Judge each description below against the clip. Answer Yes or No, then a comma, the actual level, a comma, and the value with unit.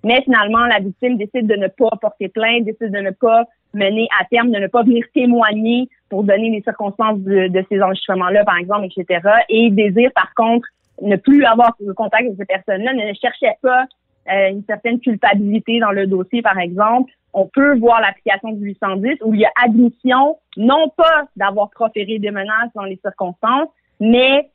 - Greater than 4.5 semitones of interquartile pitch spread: No, average, 3.3 semitones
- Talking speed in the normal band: Yes, average, 190 wpm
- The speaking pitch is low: No, high, 220 Hz